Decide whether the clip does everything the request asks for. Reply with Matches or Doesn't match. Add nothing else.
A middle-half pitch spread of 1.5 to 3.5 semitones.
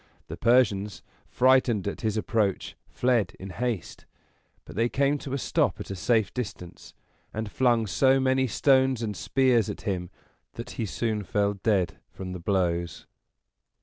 Doesn't match